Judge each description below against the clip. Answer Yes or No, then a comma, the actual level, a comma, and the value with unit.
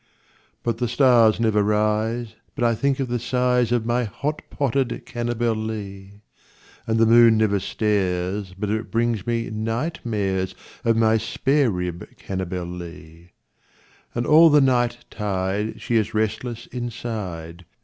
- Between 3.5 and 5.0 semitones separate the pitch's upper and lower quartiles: No, average, 3.1 semitones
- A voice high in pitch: No, low, 110 Hz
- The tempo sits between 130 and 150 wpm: Yes, average, 140 wpm